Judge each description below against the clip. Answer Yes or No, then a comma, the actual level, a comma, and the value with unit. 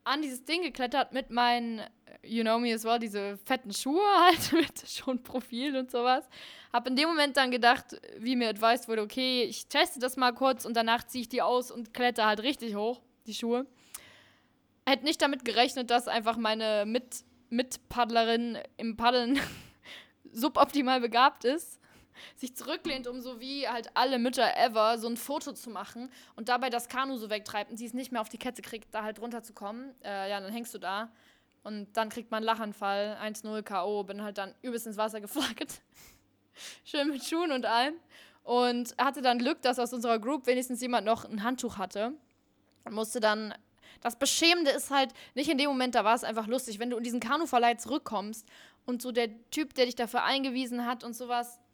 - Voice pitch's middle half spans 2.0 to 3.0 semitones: Yes, narrow, 2.5 semitones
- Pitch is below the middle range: No, high, 245 Hz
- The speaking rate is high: Yes, fast, 195 wpm